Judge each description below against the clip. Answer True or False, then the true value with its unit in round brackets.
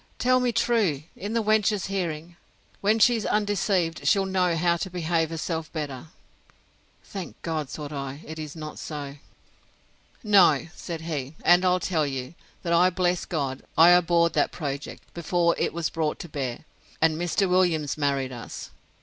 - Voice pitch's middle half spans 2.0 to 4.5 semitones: True (3.4 semitones)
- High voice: False (170 Hz)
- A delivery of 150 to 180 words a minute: True (160 wpm)